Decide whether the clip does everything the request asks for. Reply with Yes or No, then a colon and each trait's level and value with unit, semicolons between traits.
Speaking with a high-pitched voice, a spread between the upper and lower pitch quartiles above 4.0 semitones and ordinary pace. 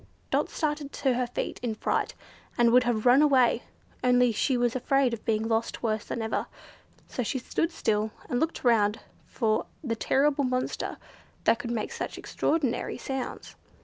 No: high, 245 Hz; average, 2.8 semitones; average, 170 wpm